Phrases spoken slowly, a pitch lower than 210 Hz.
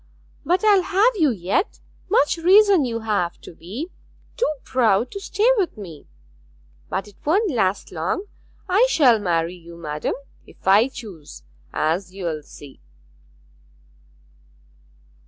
No: slow, 130 wpm; high, 225 Hz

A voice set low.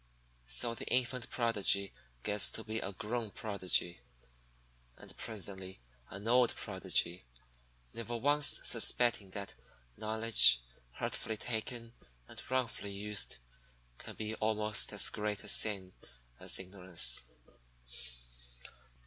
Yes: low, 105 Hz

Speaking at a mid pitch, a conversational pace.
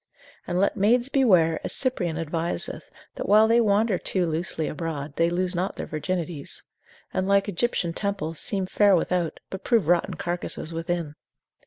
Yes: medium, 180 Hz; average, 160 wpm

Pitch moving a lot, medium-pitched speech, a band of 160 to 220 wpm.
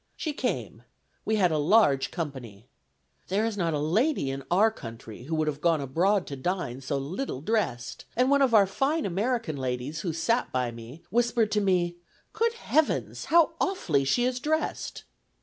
Yes: wide, 9.0 semitones; medium, 175 Hz; average, 180 wpm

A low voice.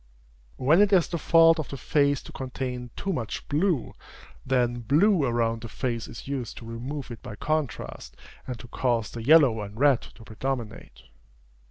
Yes: low, 130 Hz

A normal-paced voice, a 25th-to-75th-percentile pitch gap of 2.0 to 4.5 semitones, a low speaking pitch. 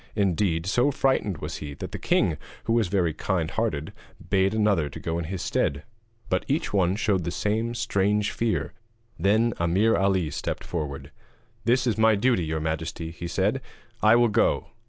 No: average, 175 wpm; average, 5.0 semitones; very low, 95 Hz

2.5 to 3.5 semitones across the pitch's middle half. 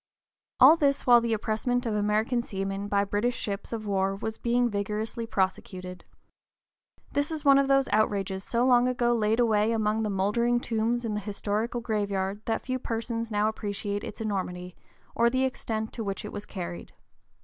Yes: average, 2.8 semitones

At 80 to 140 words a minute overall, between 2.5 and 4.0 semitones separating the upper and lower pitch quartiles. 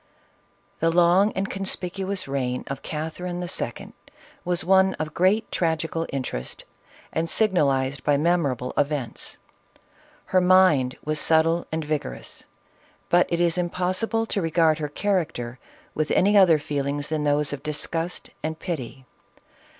Yes: slow, 135 wpm; average, 3.7 semitones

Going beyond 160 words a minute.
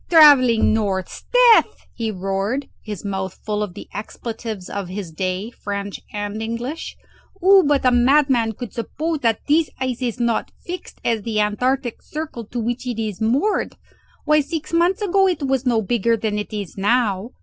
Yes: average, 175 wpm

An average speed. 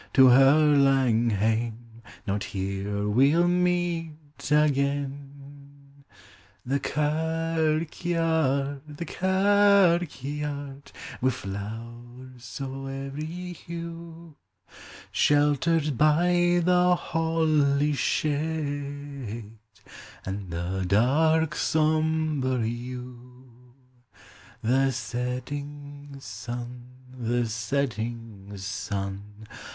No: slow, 70 wpm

